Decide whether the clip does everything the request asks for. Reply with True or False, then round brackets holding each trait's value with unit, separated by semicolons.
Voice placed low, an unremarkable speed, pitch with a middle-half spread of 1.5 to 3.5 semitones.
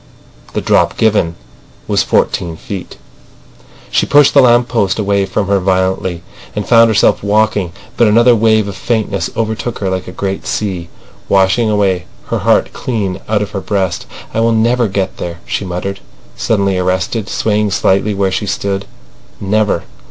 True (100 Hz; 160 wpm; 2.6 semitones)